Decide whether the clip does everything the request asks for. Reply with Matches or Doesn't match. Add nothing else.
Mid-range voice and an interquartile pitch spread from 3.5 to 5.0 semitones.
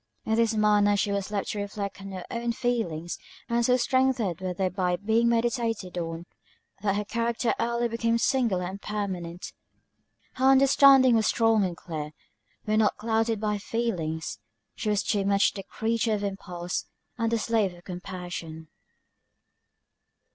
Doesn't match